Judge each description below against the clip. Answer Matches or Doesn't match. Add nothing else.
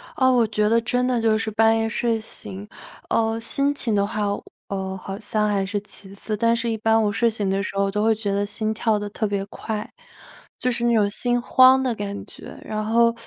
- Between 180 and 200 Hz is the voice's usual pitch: Doesn't match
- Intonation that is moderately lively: Doesn't match